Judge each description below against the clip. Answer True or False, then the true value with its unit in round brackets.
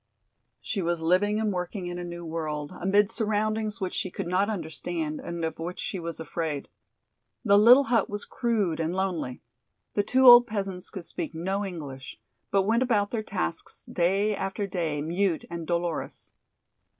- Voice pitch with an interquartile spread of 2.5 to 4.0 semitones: True (3.7 semitones)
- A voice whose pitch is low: False (185 Hz)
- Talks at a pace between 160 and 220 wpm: True (170 wpm)